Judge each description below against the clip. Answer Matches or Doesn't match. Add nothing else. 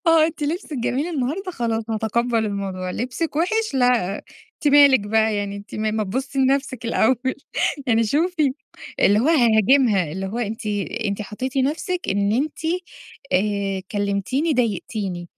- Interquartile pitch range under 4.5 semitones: Doesn't match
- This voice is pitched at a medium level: Doesn't match